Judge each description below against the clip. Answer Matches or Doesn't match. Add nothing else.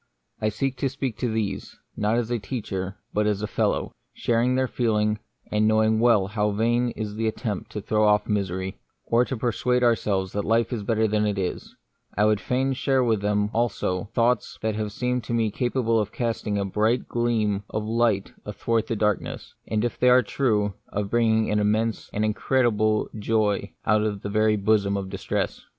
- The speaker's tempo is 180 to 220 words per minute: Matches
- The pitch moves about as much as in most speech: Doesn't match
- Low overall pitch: Matches